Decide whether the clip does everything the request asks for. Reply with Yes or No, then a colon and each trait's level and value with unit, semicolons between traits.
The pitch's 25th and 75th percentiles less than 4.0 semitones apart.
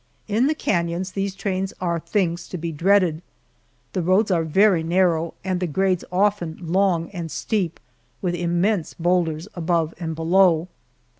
Yes: narrow, 2.5 semitones